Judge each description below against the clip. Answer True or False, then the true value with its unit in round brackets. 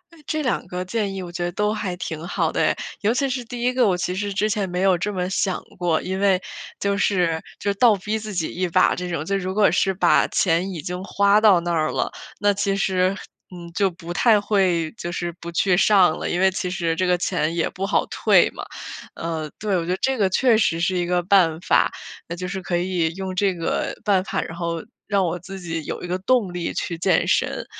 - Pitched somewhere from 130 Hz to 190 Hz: True (185 Hz)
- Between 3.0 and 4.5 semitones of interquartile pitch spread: False (2.5 semitones)